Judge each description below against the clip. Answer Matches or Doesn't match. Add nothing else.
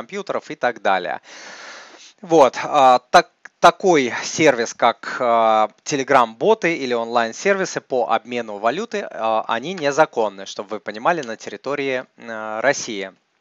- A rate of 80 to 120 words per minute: Matches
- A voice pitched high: Doesn't match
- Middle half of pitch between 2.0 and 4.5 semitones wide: Doesn't match